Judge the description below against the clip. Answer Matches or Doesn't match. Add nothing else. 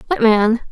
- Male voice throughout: Doesn't match